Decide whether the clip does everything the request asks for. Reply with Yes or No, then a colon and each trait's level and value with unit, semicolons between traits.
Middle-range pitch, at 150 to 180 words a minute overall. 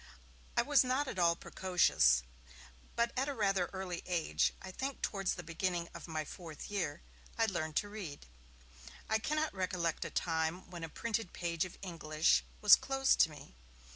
Yes: medium, 180 Hz; average, 170 wpm